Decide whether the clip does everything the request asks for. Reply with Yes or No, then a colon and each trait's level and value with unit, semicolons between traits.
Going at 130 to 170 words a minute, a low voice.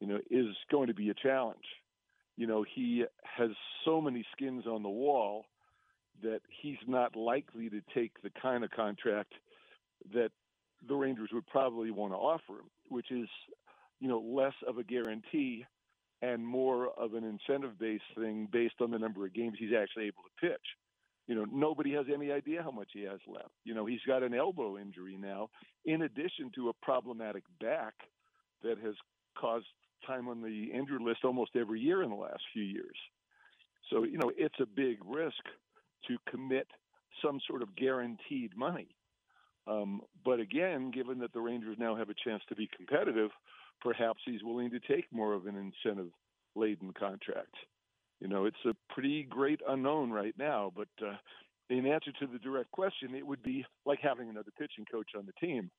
No: average, 180 wpm; low, 120 Hz